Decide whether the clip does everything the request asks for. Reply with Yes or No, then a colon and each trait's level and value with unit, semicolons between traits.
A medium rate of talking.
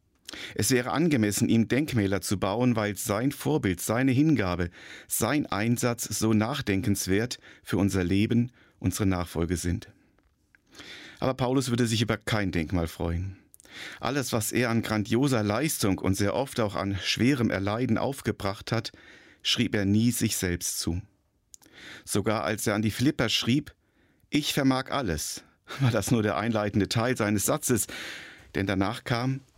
Yes: average, 145 wpm